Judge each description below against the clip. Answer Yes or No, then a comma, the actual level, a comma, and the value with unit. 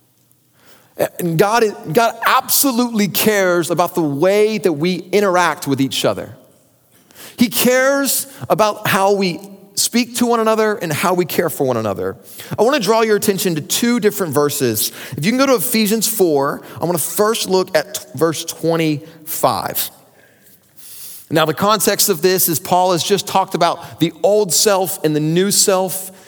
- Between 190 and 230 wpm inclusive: No, average, 170 wpm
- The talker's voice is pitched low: No, medium, 185 Hz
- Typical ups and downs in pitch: Yes, average, 4.9 semitones